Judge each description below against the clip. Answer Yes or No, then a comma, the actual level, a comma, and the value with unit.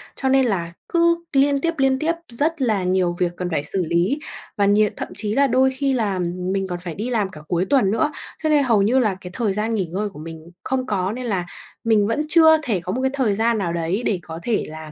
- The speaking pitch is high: Yes, high, 215 Hz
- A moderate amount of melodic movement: No, wide, 6.4 semitones